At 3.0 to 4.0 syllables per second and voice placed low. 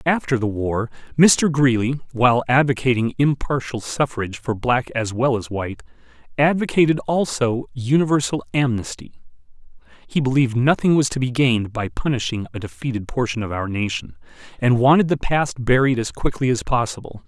No: 5.4 syllables/s; low, 125 Hz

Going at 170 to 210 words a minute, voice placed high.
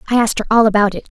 No: fast, 315 wpm; high, 220 Hz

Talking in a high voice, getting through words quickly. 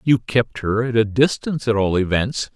No: low, 115 Hz; fast, 210 wpm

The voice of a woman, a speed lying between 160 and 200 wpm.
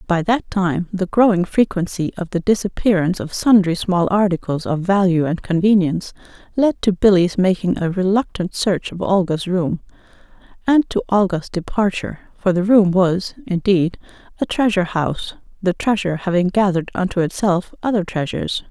No: female; average, 150 wpm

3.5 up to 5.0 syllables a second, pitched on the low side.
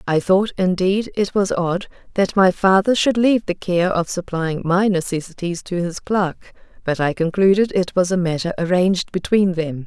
No: 4.8 syllables/s; medium, 185 Hz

